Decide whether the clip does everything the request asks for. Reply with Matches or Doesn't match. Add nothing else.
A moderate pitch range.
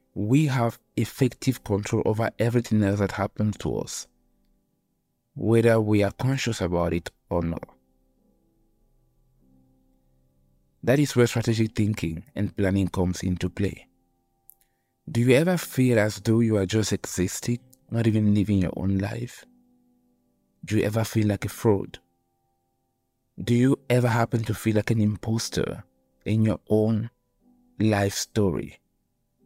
Matches